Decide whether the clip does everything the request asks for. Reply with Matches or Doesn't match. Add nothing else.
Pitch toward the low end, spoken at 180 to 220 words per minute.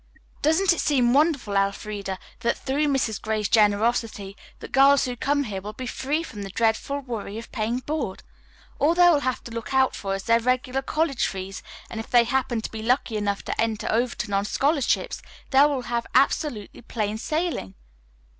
Doesn't match